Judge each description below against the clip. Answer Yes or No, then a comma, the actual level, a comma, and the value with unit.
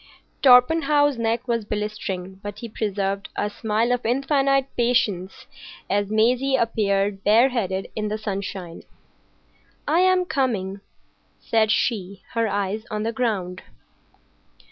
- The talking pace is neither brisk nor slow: No, slow, 120 wpm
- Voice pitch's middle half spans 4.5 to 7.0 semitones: No, average, 3.8 semitones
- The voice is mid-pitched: No, high, 220 Hz